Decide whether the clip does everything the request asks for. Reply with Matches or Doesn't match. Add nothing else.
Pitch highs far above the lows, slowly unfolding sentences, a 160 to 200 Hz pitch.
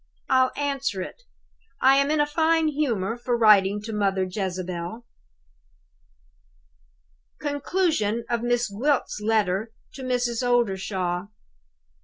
Doesn't match